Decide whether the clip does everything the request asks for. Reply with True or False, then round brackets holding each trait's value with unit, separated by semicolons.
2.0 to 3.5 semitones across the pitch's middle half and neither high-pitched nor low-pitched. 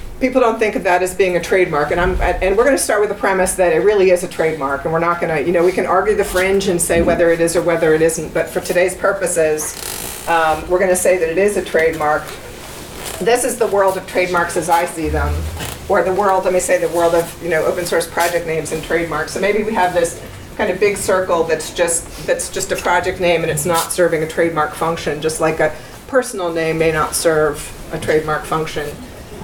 True (2.5 semitones; 175 Hz)